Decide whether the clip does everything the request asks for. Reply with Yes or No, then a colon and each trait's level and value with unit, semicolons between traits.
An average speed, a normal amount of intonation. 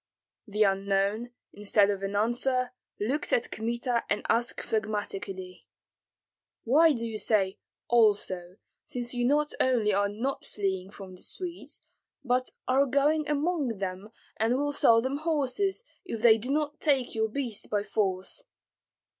Yes: average, 145 wpm; average, 5.0 semitones